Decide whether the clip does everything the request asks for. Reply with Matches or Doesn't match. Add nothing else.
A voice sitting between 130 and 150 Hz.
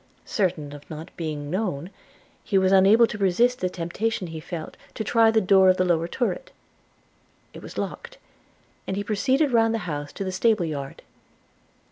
Doesn't match